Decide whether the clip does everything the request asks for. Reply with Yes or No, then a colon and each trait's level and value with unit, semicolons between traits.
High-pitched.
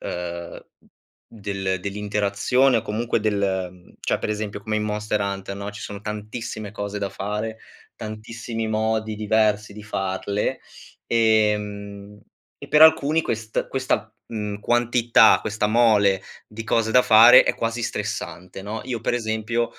No: low, 105 Hz